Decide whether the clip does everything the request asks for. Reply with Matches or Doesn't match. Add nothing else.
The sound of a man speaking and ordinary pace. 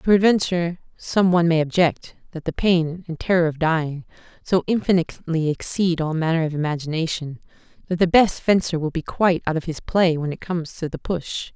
Doesn't match